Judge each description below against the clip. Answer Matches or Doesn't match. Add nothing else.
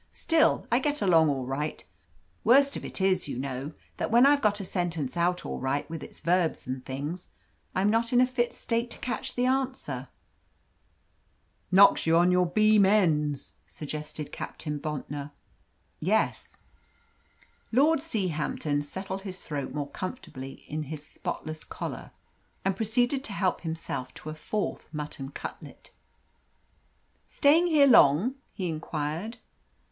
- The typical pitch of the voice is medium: Matches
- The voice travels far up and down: Matches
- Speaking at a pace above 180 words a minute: Doesn't match